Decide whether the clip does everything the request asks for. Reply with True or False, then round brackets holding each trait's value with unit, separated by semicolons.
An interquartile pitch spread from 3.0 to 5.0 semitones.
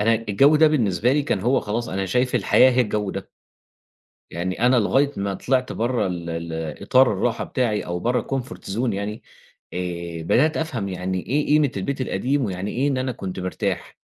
False (5.6 semitones)